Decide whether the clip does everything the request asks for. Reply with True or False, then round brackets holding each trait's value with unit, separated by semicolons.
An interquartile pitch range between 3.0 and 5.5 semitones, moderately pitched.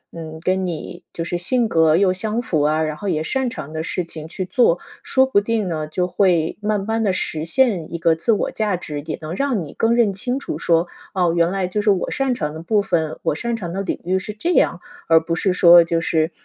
True (4.5 semitones; 180 Hz)